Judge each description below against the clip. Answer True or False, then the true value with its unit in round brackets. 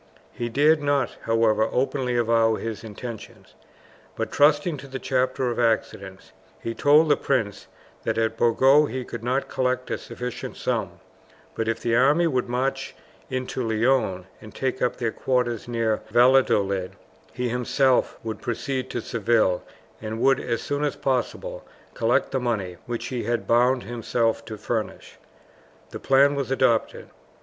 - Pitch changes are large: False (2.8 semitones)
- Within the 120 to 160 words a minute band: True (155 wpm)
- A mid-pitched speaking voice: False (120 Hz)